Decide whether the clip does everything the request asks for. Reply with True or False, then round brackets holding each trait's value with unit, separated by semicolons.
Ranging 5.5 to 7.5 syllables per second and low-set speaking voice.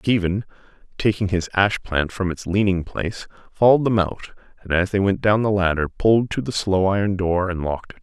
True (5.6 syllables/s; 95 Hz)